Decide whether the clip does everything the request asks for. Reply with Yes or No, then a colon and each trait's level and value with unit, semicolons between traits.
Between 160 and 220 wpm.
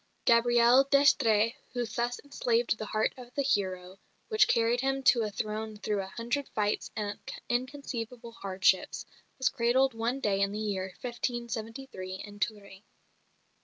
No: average, 145 wpm